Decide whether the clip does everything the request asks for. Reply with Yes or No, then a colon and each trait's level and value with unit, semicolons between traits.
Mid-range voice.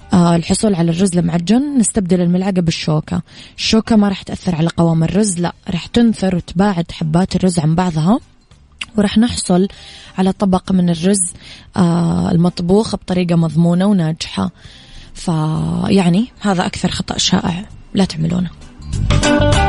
Yes: medium, 180 Hz